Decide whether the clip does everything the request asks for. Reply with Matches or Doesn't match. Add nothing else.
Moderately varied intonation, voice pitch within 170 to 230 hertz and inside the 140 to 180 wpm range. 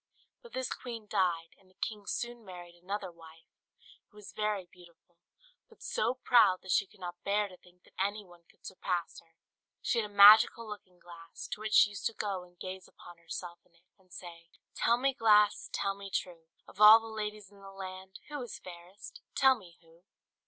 Doesn't match